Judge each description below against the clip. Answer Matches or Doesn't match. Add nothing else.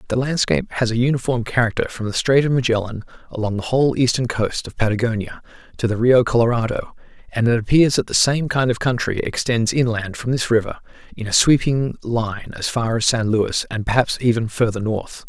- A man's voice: Matches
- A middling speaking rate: Matches